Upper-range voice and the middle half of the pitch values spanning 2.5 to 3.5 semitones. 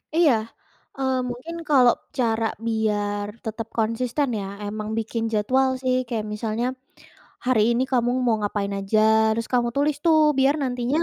Yes: high, 235 Hz; average, 3.1 semitones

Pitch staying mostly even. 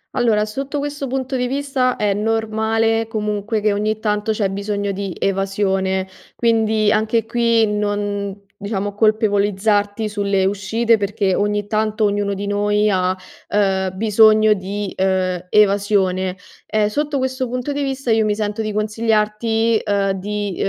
Yes: narrow, 1.9 semitones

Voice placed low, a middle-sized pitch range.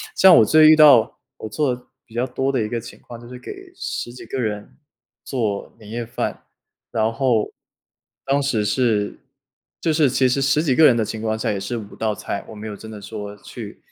Yes: low, 120 Hz; average, 3.8 semitones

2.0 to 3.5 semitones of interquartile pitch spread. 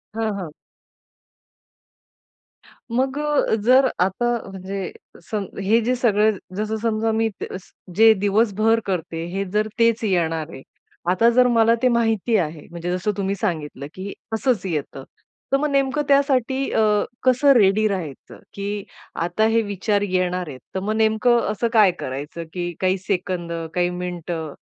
No: average, 4.1 semitones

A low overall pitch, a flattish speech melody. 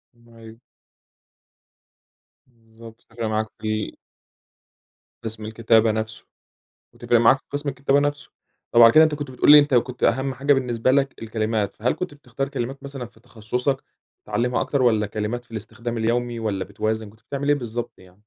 No: low, 120 Hz; average, 3.3 semitones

